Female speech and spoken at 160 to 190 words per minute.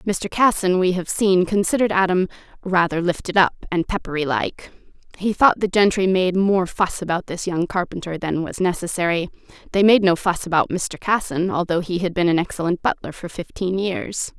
Yes: female; average, 185 wpm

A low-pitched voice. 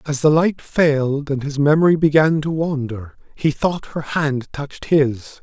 No: medium, 145 Hz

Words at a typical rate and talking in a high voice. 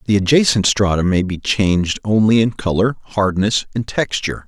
No: average, 160 wpm; low, 105 Hz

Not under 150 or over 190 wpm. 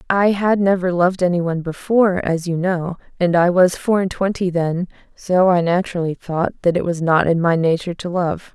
No: fast, 205 wpm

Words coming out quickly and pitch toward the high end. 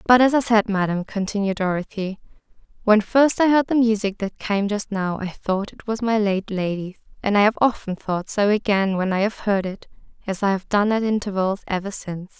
Yes: fast, 215 wpm; high, 205 Hz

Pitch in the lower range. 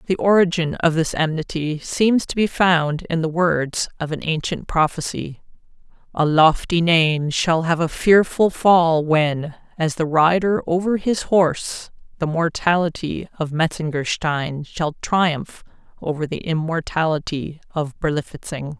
No: medium, 165 Hz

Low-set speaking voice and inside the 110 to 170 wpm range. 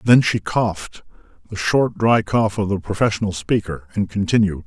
Yes: low, 100 Hz; average, 140 wpm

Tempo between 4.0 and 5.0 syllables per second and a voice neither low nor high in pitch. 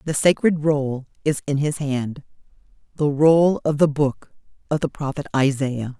Yes: 4.3 syllables/s; medium, 145 Hz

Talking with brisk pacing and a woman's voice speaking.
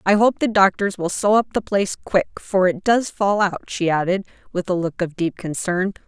Yes: fast, 225 wpm; female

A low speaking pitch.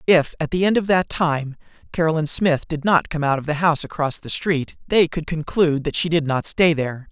No: medium, 160 Hz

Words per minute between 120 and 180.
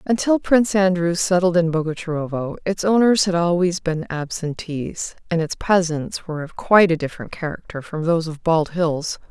Yes: average, 170 wpm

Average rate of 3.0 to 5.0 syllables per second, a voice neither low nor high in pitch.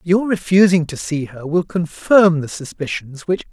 Yes: 4.5 syllables/s; medium, 165 Hz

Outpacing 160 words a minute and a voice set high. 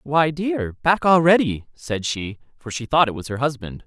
No: average, 200 wpm; low, 135 Hz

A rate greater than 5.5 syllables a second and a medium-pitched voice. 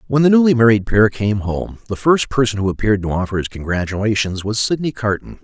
No: 6.0 syllables/s; low, 110 Hz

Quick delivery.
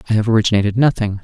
No: average, 195 wpm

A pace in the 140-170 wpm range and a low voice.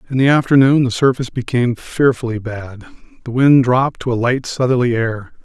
Yes: average, 165 wpm; low, 125 Hz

